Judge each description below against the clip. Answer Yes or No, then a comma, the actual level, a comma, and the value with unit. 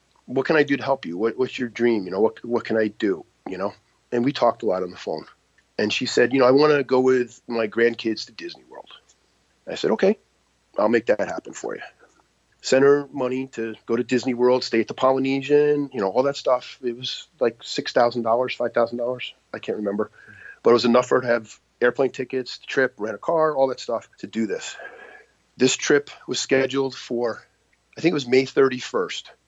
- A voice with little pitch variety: Yes, narrow, 2.2 semitones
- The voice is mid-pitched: No, low, 125 Hz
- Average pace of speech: No, fast, 230 wpm